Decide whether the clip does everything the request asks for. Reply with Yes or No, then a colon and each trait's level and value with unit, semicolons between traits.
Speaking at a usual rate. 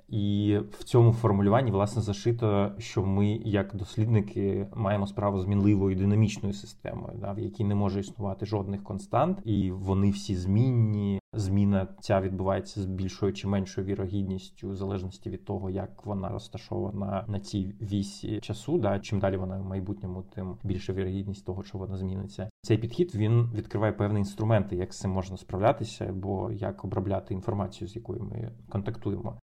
No: fast, 160 wpm